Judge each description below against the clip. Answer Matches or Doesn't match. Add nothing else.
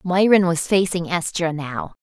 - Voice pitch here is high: Doesn't match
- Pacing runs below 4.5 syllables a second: Matches